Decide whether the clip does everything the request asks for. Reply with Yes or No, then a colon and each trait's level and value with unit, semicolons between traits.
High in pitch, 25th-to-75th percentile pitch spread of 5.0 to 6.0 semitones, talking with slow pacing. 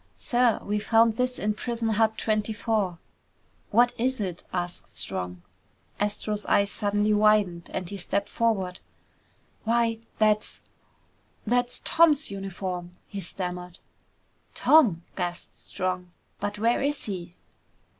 No: high, 210 Hz; average, 3.7 semitones; slow, 120 wpm